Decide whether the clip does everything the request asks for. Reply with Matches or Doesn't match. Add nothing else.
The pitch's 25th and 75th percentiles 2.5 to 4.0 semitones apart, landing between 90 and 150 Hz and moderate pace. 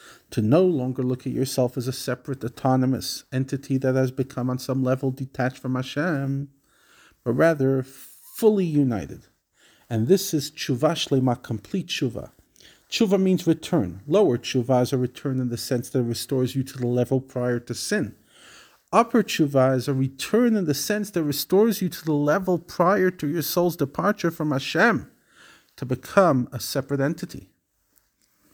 Doesn't match